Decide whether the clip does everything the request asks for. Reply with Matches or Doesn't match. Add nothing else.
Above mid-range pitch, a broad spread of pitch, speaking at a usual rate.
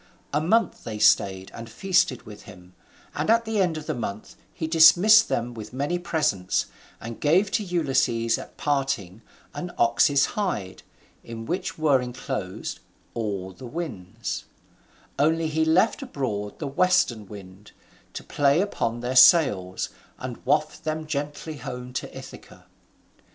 Doesn't match